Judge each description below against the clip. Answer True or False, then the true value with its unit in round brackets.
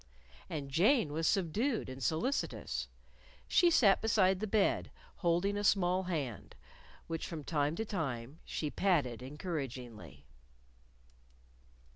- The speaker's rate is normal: False (115 wpm)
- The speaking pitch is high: False (165 Hz)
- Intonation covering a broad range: True (6.2 semitones)